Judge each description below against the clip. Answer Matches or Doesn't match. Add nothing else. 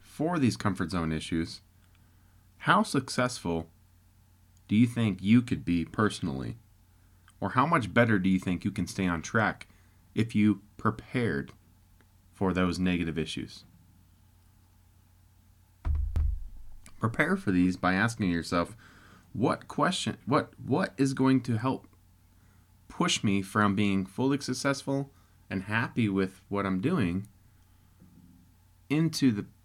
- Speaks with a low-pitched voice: Matches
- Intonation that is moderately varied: Matches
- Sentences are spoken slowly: Matches